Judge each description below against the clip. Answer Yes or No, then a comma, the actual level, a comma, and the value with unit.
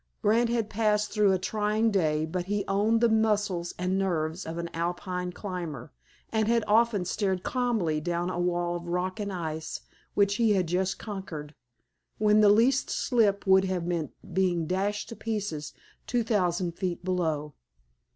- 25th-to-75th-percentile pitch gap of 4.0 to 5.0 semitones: No, average, 3.4 semitones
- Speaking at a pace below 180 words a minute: Yes, average, 165 wpm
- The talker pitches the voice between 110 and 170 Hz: No, high, 190 Hz